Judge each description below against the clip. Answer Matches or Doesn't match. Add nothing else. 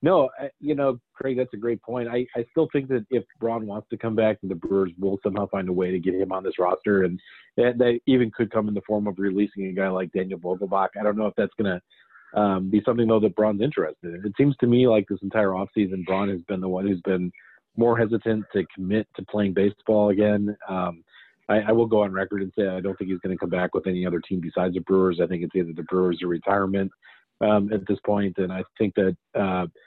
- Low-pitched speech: Matches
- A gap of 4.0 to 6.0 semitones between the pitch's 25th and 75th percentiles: Doesn't match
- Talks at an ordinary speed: Doesn't match